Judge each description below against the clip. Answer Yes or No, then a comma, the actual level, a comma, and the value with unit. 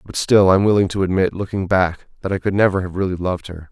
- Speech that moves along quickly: Yes, fast, 275 wpm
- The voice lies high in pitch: No, very low, 95 Hz